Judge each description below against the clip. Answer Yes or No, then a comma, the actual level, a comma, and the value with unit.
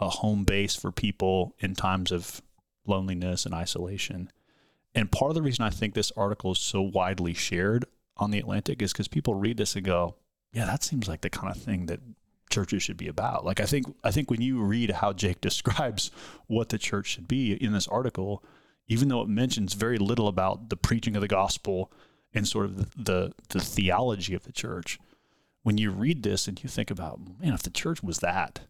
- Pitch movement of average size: Yes, average, 3.3 semitones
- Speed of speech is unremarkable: No, fast, 215 wpm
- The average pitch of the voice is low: Yes, low, 105 Hz